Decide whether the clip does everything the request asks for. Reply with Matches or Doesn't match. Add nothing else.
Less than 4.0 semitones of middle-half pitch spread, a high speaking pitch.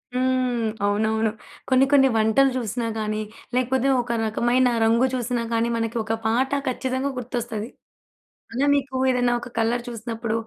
Matches